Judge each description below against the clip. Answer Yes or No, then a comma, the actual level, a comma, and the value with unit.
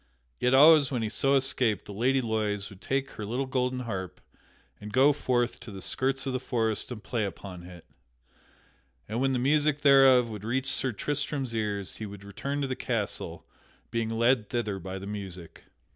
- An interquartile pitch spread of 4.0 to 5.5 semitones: Yes, average, 4.4 semitones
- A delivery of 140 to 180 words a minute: No, average, 190 wpm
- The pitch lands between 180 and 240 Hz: No, low, 120 Hz